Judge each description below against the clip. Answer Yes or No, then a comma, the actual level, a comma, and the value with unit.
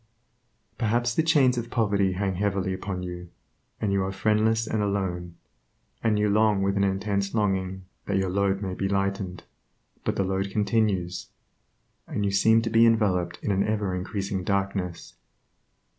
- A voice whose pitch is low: Yes, low, 100 Hz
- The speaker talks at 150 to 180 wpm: Yes, average, 160 wpm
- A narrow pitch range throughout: Yes, narrow, 2.2 semitones